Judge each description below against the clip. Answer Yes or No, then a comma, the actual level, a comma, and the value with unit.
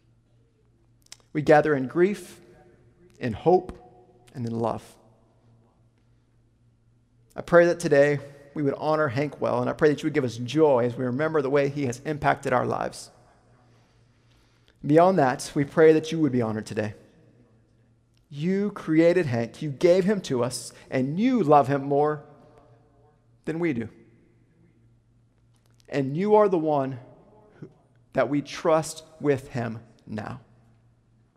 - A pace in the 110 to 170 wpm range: Yes, average, 140 wpm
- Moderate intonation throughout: Yes, average, 4.4 semitones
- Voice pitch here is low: Yes, low, 125 Hz